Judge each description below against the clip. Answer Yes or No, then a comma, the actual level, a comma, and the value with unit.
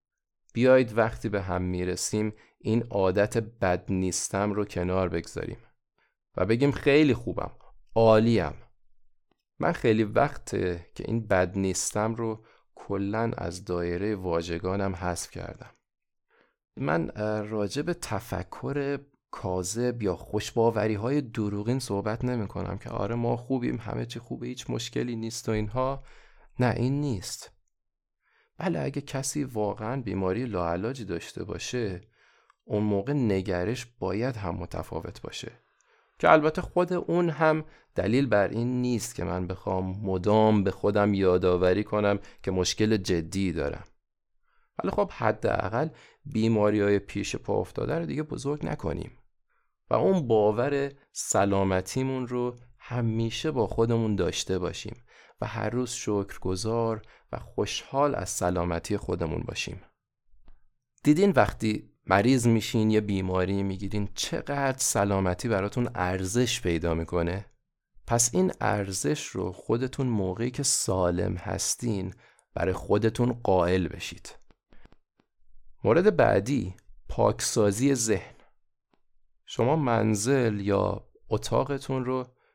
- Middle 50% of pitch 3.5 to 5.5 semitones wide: Yes, average, 4.6 semitones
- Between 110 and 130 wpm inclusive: Yes, average, 120 wpm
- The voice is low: Yes, low, 105 Hz